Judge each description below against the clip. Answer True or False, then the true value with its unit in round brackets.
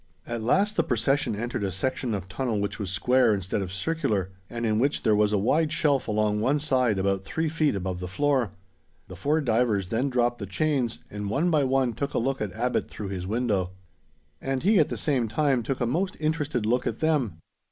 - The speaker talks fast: True (215 wpm)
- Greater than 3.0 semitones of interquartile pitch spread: True (5.5 semitones)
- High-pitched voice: False (120 Hz)